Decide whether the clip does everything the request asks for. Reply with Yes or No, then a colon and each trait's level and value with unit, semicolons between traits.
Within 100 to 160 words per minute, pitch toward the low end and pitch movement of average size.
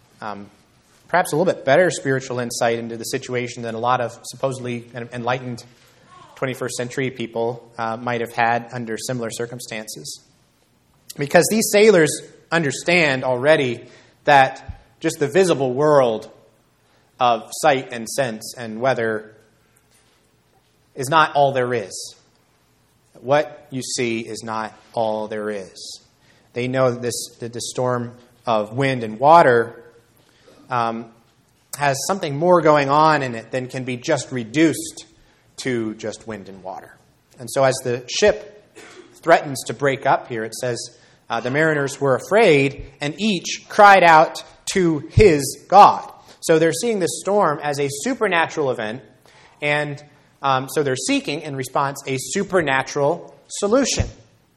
Yes: average, 140 wpm; low, 130 Hz; average, 4.4 semitones